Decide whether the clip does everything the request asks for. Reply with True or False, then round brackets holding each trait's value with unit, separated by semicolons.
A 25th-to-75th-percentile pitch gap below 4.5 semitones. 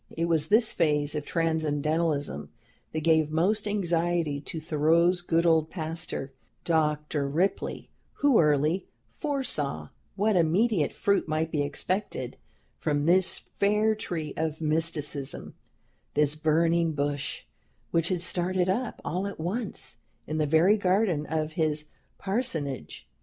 True (3.4 semitones)